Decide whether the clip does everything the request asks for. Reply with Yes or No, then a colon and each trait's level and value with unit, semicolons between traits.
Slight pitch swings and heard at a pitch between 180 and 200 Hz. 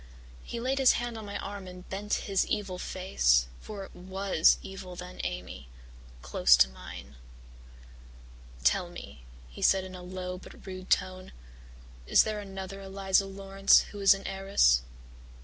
Yes: narrow, 1.6 semitones; high, 190 Hz